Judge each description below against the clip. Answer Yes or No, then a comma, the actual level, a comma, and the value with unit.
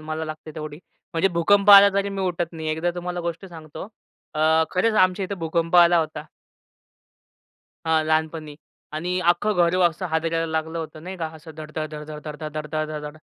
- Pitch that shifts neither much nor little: No, narrow, 2.3 semitones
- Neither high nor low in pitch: Yes, medium, 160 Hz